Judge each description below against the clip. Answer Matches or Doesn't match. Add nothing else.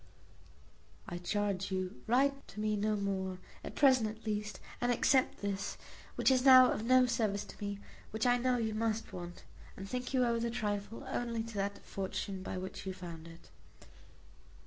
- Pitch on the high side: Matches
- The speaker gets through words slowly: Doesn't match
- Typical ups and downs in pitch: Matches